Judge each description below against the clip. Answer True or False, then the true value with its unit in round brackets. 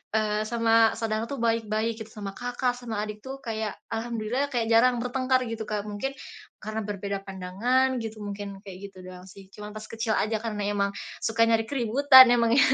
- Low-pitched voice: False (225 Hz)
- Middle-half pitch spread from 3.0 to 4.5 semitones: False (2.4 semitones)